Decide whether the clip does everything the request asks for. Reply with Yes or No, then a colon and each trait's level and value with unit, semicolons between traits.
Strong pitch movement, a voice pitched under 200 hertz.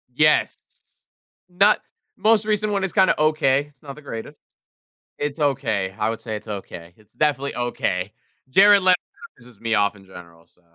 Yes: wide, 6.9 semitones; low, 135 Hz